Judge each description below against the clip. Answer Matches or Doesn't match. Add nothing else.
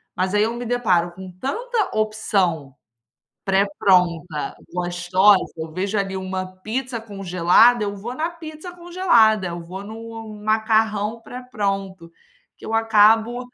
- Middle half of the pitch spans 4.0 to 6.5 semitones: Doesn't match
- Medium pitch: Doesn't match